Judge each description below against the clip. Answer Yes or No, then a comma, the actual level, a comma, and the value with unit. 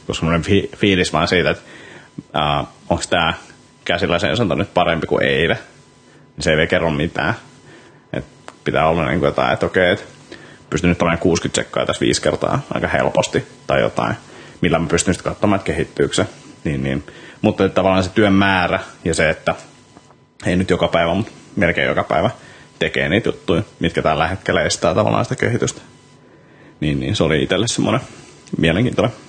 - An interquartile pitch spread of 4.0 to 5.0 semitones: No, average, 3.6 semitones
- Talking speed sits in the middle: No, fast, 170 wpm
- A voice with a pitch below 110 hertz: Yes, very low, 85 Hz